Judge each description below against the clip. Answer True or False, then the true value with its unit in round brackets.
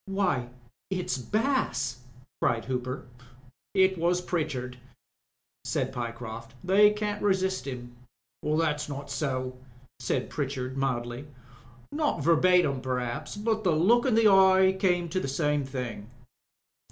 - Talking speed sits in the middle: False (120 wpm)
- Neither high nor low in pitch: True (150 Hz)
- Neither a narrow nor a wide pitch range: False (6.9 semitones)